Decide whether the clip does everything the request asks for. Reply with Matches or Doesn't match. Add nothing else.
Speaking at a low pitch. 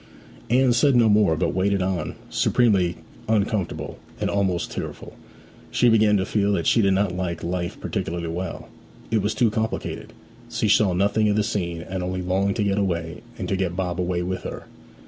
Matches